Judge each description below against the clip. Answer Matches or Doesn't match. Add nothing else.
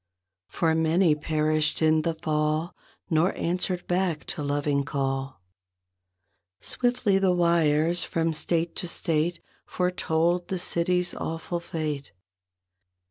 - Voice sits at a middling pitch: Matches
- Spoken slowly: Matches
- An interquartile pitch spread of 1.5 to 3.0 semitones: Matches